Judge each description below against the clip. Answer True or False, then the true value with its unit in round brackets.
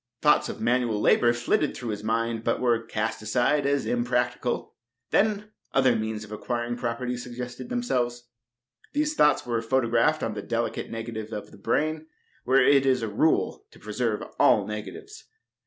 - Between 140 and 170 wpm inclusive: True (160 wpm)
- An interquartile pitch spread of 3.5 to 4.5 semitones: False (2.8 semitones)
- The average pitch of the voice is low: True (120 Hz)